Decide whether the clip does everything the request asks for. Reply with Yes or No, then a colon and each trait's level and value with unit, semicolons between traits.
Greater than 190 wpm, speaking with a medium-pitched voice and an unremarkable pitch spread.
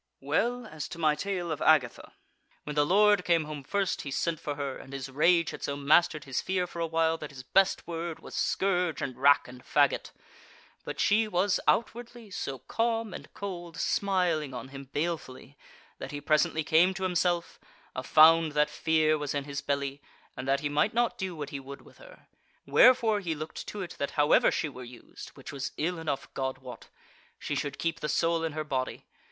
Yes: fast, 205 wpm; medium, 155 Hz; average, 4.1 semitones